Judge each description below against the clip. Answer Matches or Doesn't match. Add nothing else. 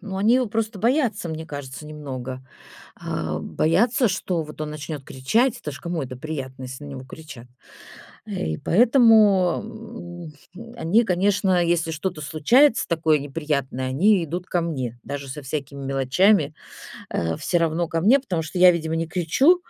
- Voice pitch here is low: Doesn't match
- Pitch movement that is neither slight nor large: Doesn't match